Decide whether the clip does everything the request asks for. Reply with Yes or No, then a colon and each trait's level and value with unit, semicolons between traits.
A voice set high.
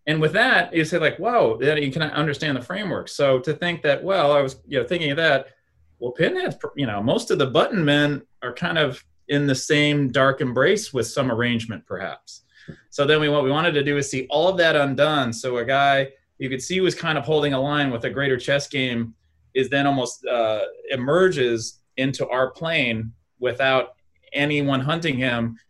No: medium, 140 Hz